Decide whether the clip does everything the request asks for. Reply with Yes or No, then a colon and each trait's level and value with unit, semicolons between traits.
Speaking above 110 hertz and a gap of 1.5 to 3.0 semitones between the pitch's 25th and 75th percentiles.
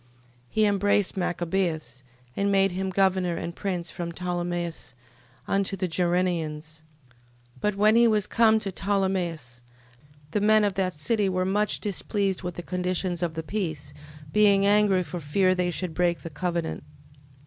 Yes: medium, 185 Hz; narrow, 2.6 semitones